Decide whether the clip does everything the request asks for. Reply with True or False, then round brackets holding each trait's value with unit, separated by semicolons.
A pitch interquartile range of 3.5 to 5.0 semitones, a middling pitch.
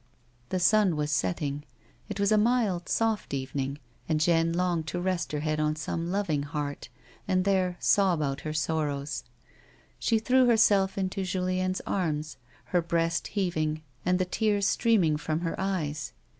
True (4.0 semitones; 175 Hz)